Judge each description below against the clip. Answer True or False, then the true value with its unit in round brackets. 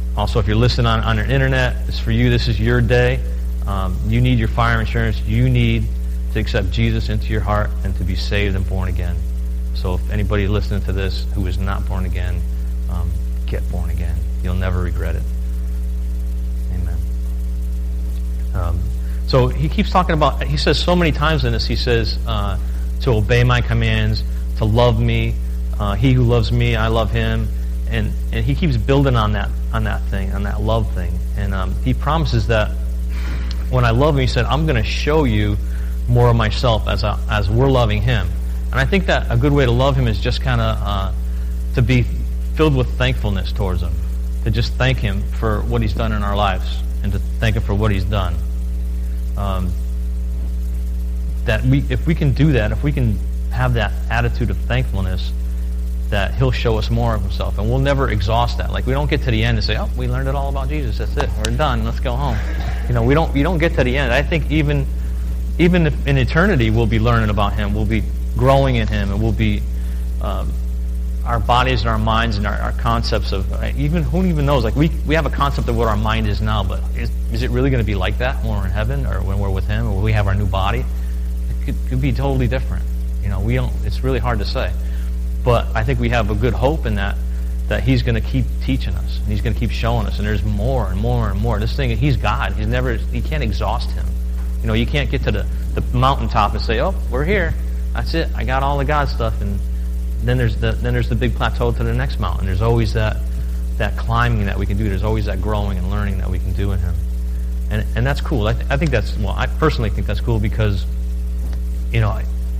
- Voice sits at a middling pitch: False (85 Hz)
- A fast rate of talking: True (230 wpm)